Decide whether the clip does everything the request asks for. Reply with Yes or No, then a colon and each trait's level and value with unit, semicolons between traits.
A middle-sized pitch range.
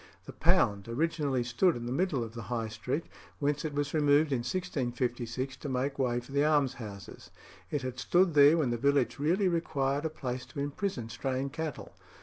Yes: average, 3.6 semitones